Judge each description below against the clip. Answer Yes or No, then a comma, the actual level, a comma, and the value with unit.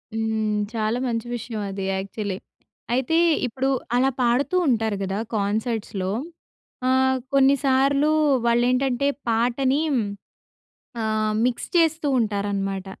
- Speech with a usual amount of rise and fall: Yes, average, 3.7 semitones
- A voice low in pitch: No, high, 235 Hz